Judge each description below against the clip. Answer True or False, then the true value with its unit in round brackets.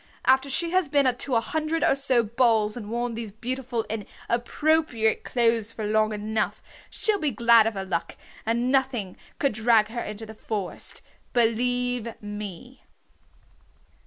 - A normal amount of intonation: True (3.1 semitones)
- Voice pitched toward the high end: True (235 Hz)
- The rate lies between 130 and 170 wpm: True (150 wpm)